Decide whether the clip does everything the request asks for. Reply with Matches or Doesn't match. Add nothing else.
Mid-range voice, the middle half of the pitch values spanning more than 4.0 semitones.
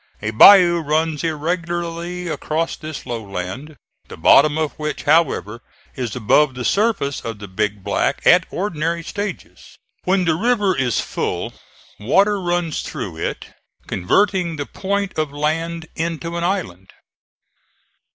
Matches